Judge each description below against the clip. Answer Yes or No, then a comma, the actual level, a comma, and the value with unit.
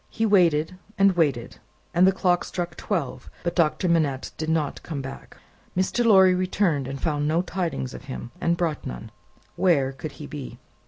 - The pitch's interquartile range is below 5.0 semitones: Yes, average, 4.4 semitones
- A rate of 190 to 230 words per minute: No, average, 175 wpm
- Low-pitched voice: No, medium, 165 Hz